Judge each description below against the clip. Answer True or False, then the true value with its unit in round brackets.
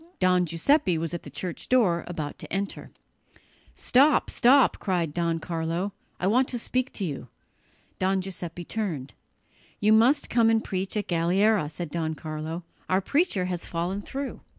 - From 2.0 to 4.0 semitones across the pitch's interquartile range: False (4.8 semitones)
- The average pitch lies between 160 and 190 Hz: True (185 Hz)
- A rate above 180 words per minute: False (160 wpm)